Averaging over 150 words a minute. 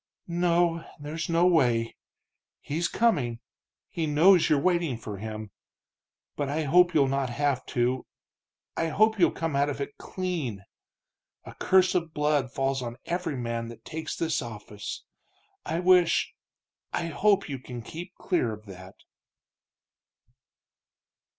No: slow, 135 wpm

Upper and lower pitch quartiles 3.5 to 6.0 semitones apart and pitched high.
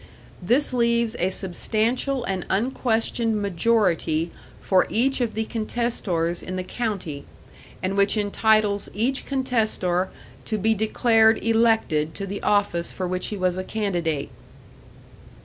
Yes: average, 3.8 semitones; high, 210 Hz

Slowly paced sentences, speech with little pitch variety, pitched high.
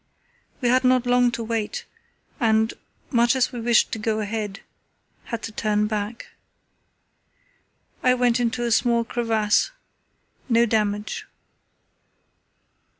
Yes: slow, 120 wpm; narrow, 1.9 semitones; high, 230 Hz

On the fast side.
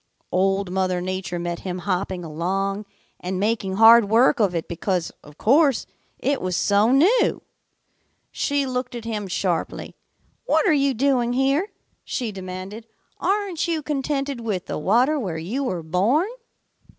No: average, 150 wpm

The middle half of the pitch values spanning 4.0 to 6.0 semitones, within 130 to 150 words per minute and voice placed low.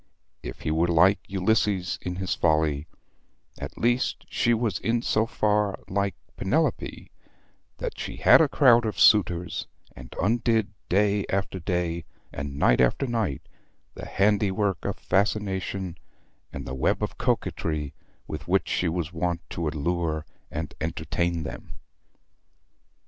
Yes: average, 4.3 semitones; slow, 135 wpm; very low, 90 Hz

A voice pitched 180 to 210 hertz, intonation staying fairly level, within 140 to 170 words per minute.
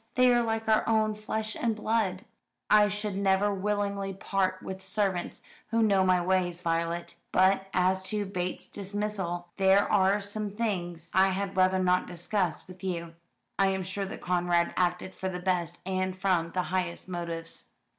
Yes: high, 190 Hz; narrow, 2.2 semitones; average, 165 wpm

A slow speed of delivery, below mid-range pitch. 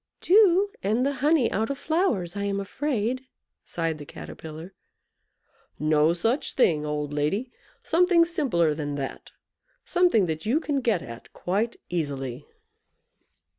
No: slow, 130 wpm; high, 200 Hz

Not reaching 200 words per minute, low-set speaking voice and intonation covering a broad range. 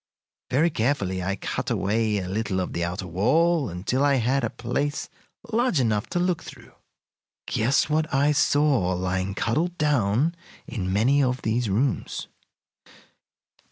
Yes: average, 145 wpm; low, 120 Hz; wide, 6.8 semitones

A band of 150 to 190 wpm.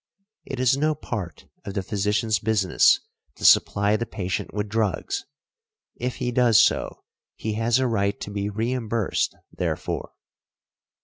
No: average, 140 wpm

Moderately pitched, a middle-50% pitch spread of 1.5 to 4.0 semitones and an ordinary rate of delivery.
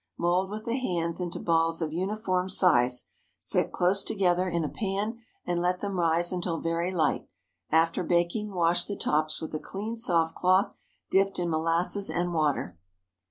Yes: medium, 175 Hz; narrow, 2.6 semitones; average, 165 wpm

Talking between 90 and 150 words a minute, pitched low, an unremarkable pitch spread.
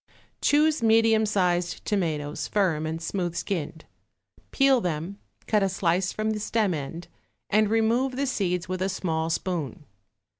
No: average, 145 wpm; high, 190 Hz; average, 4.6 semitones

